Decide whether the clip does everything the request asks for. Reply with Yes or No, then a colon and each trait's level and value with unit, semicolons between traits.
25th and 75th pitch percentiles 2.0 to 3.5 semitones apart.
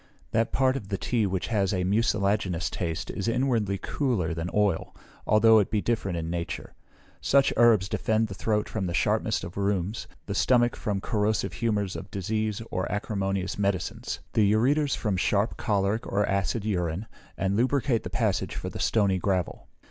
Yes: average, 2.8 semitones